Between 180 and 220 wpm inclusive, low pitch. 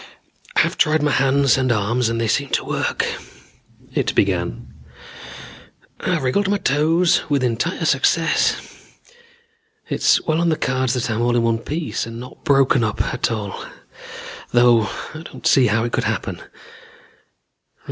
No: average, 150 wpm; low, 130 Hz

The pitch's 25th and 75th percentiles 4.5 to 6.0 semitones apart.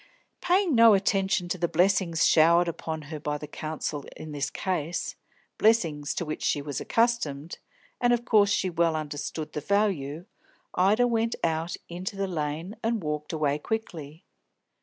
Yes: average, 5.0 semitones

